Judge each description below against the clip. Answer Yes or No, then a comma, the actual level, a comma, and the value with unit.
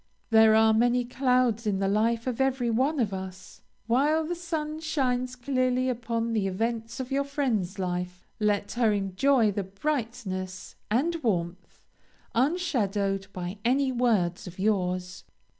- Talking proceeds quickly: No, average, 140 wpm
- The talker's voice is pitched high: Yes, high, 230 Hz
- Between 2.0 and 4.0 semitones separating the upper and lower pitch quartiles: No, average, 4.7 semitones